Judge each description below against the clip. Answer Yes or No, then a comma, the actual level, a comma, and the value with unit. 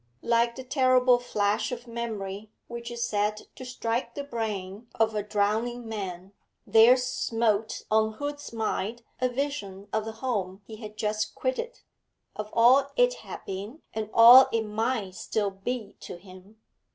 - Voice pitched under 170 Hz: No, high, 225 Hz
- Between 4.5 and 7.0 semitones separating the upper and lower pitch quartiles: No, average, 3.0 semitones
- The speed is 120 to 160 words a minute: Yes, average, 155 wpm